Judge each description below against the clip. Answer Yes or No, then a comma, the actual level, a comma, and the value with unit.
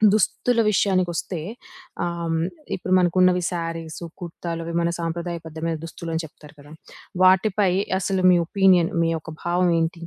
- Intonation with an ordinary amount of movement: No, narrow, 1.8 semitones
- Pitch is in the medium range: Yes, medium, 170 Hz